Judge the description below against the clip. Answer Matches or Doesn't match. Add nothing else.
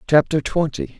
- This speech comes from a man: Matches